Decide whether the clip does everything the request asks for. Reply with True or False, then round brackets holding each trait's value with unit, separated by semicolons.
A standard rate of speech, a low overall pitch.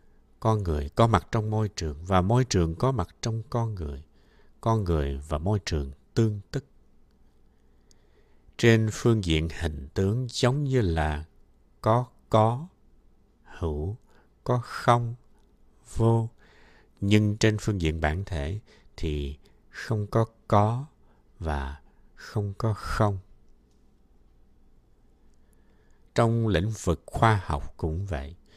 False (120 wpm; 100 Hz)